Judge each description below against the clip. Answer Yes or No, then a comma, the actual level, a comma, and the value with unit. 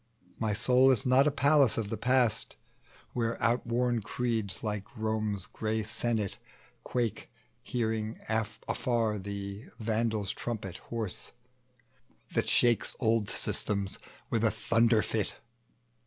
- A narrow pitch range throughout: Yes, narrow, 2.0 semitones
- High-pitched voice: No, low, 110 Hz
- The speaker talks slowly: Yes, slow, 115 wpm